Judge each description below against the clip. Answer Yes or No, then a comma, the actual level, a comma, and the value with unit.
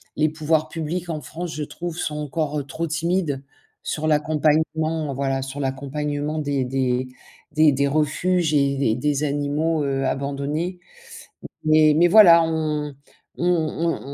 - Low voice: No, medium, 150 Hz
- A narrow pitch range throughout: Yes, narrow, 2.3 semitones